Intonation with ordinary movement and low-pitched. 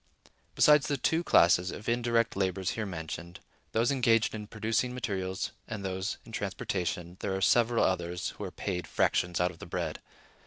Yes: average, 4.3 semitones; low, 100 Hz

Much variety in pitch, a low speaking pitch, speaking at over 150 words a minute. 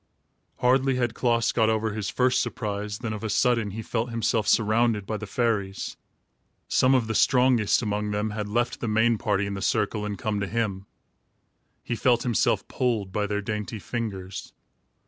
No: narrow, 2.4 semitones; low, 110 Hz; average, 180 wpm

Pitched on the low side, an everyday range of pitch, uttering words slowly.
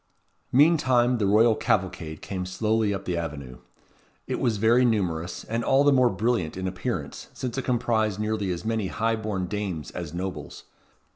No: low, 105 Hz; average, 4.2 semitones; average, 165 wpm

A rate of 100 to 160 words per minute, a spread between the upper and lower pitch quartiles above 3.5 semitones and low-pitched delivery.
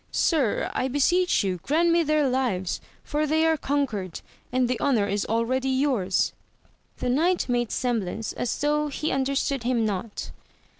No: average, 155 wpm; average, 4.7 semitones; very high, 260 Hz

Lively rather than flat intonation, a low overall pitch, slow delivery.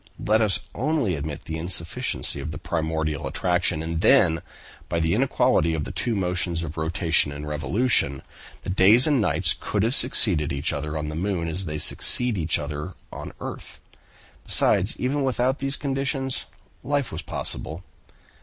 No: wide, 7.0 semitones; very low, 85 Hz; average, 165 wpm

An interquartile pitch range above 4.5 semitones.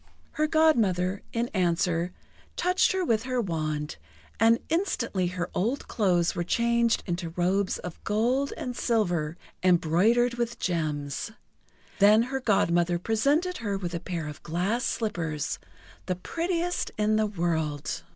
Yes: wide, 5.5 semitones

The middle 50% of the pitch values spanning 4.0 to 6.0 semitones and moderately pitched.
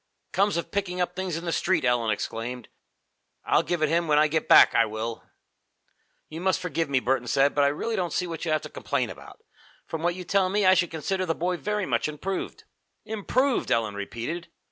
Yes: average, 5.3 semitones; medium, 165 Hz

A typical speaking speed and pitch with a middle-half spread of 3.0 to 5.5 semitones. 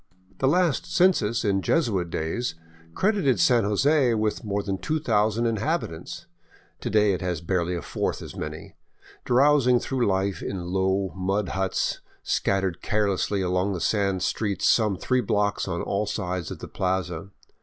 Yes: average, 155 wpm; average, 4.2 semitones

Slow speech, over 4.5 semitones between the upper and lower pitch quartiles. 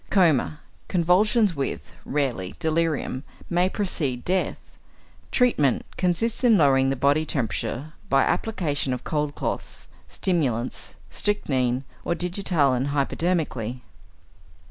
Yes: slow, 100 wpm; average, 5.2 semitones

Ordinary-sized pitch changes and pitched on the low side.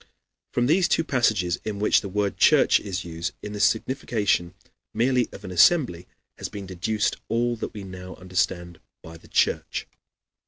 Yes: average, 4.2 semitones; low, 100 Hz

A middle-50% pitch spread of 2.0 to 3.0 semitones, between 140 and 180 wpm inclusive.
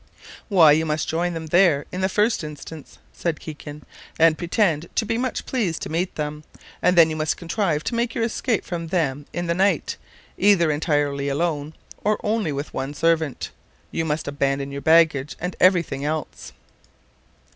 No: average, 3.4 semitones; average, 175 wpm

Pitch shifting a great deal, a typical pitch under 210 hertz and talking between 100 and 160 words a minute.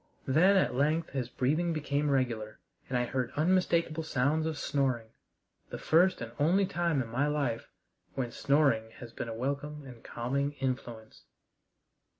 No: average, 4.2 semitones; medium, 140 Hz; average, 155 wpm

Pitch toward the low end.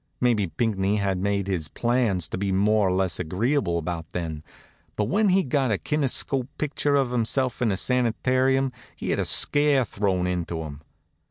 Yes: low, 105 Hz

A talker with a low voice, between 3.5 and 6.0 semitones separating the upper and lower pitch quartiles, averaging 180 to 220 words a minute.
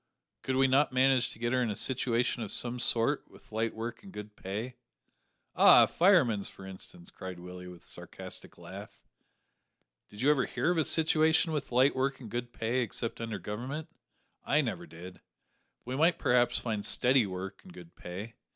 Yes: low, 120 Hz; average, 4.5 semitones; average, 190 wpm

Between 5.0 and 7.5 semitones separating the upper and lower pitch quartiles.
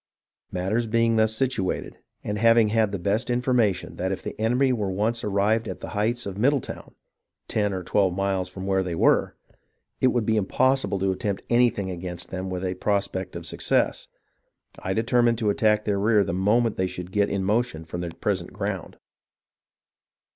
No: average, 3.5 semitones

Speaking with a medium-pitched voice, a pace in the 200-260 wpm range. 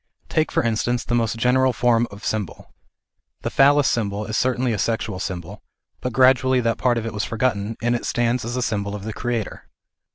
No: low, 115 Hz; fast, 205 wpm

